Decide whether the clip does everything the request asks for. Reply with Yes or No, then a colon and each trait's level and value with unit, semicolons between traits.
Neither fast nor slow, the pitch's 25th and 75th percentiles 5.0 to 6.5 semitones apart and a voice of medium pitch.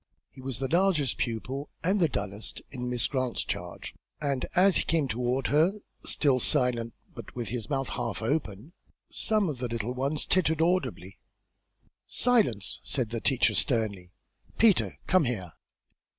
No: average, 150 wpm; average, 5.3 semitones; low, 130 Hz